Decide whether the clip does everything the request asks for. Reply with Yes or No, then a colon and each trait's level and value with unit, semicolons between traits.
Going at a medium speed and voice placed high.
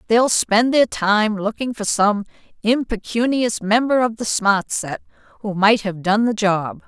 Yes: average, 165 wpm; high, 215 Hz